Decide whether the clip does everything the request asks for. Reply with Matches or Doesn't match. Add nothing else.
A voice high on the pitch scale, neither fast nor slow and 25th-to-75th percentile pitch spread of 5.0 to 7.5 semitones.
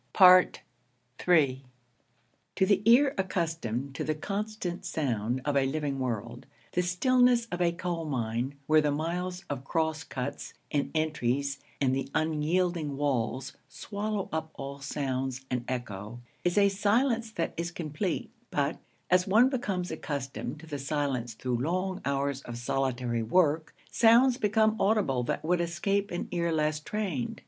Doesn't match